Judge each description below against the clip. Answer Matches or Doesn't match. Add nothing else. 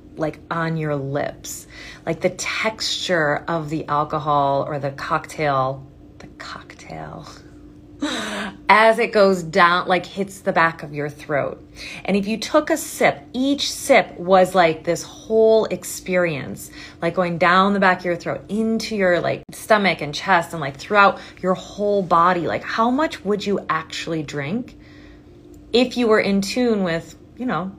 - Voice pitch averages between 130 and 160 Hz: Doesn't match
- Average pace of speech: Matches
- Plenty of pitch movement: Doesn't match